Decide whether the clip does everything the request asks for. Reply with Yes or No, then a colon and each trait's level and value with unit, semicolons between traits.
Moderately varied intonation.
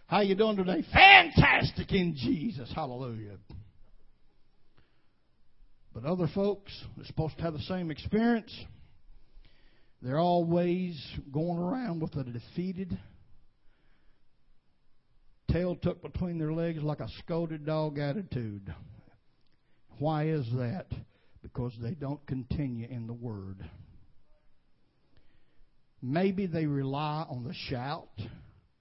No: wide, 6.8 semitones